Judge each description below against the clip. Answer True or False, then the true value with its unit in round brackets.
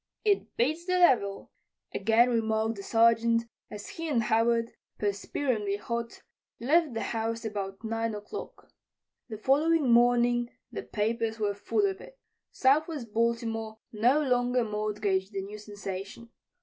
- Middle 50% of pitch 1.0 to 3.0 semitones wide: True (2.7 semitones)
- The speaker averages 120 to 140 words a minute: True (135 wpm)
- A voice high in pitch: True (230 Hz)